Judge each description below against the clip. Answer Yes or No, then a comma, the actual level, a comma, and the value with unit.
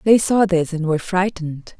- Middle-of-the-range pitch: Yes, medium, 180 Hz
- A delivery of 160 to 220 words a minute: Yes, average, 200 wpm